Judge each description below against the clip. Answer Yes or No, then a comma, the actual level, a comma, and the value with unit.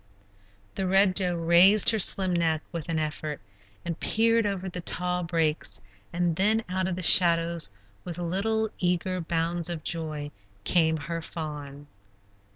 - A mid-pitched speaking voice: Yes, medium, 175 Hz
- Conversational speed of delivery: Yes, average, 150 wpm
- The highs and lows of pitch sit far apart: No, narrow, 2.5 semitones